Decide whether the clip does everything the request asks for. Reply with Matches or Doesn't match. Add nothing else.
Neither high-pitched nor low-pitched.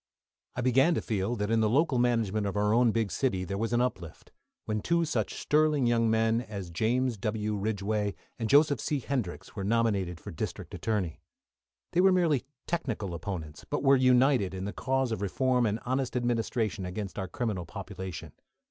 Doesn't match